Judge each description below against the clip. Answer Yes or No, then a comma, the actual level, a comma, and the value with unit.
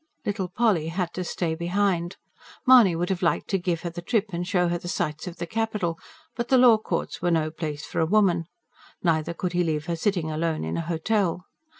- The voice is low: No, medium, 175 Hz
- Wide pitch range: No, average, 2.9 semitones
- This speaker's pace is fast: Yes, fast, 220 wpm